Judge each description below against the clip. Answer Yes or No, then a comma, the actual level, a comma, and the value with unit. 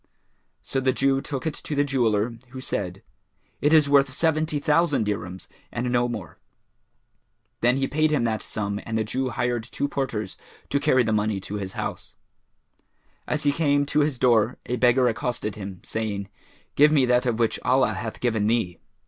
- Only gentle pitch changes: No, average, 4.6 semitones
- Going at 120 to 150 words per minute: No, average, 180 wpm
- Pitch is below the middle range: Yes, low, 125 Hz